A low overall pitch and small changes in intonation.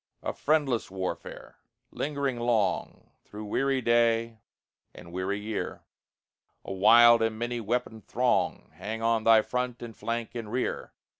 Yes: low, 115 Hz; narrow, 1.9 semitones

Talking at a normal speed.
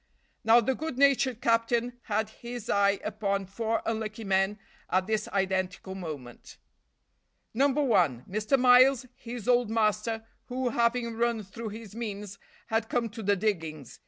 Yes: average, 145 wpm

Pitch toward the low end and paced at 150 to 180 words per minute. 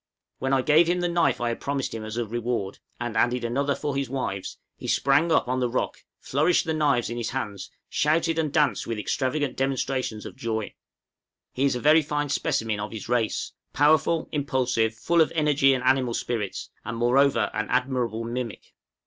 No: low, 130 Hz; average, 190 wpm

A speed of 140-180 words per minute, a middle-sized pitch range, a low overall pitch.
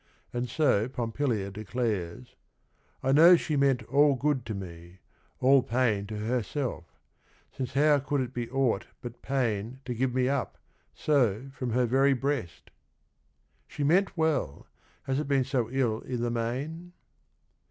Yes: average, 155 wpm; average, 3.5 semitones; low, 125 Hz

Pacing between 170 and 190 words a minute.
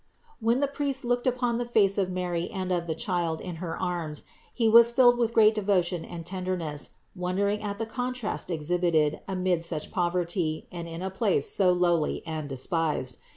Yes: average, 180 wpm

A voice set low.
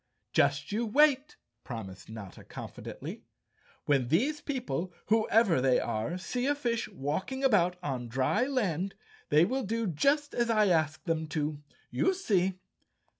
No: medium, 185 Hz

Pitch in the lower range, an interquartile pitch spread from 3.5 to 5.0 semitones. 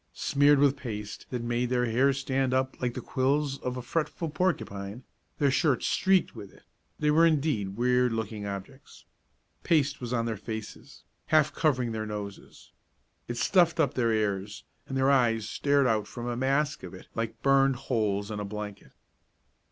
Yes: low, 125 Hz; average, 4.2 semitones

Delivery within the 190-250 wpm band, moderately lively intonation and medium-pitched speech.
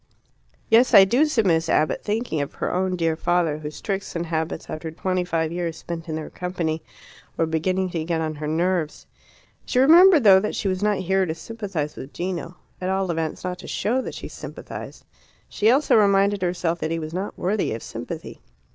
Yes: average, 200 wpm; average, 3.4 semitones; medium, 180 Hz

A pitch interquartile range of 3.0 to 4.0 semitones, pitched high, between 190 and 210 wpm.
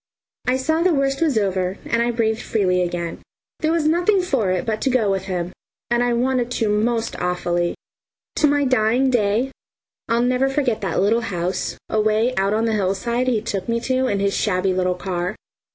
No: average, 4.8 semitones; high, 225 Hz; average, 195 wpm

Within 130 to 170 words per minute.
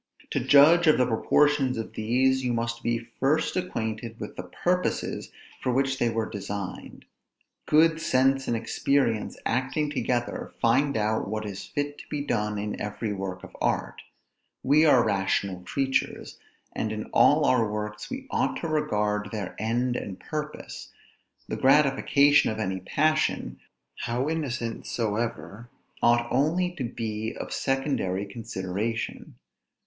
Yes: average, 145 wpm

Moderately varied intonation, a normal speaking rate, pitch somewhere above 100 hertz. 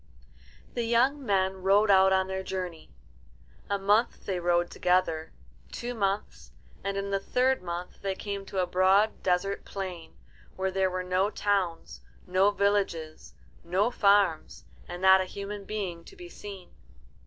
No: narrow, 1.9 semitones; average, 155 wpm; high, 190 Hz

